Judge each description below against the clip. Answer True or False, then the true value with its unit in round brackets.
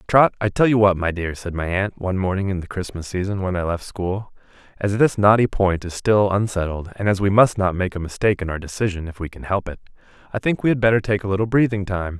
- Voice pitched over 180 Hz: False (100 Hz)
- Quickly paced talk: True (260 wpm)